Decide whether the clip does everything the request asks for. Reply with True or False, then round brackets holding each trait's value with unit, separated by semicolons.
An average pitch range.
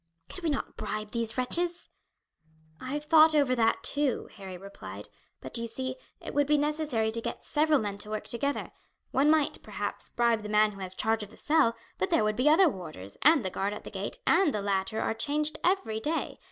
False (6.0 semitones)